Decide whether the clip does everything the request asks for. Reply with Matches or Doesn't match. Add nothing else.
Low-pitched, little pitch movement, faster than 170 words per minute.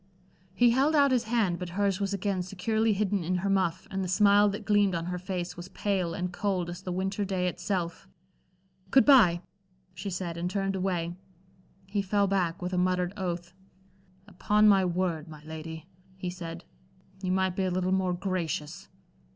Doesn't match